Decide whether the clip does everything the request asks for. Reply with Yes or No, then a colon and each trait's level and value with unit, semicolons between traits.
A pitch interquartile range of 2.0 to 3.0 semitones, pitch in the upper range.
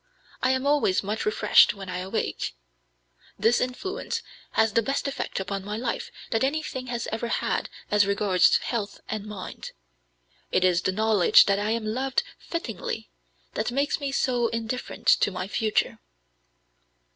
No: average, 4.3 semitones; high, 220 Hz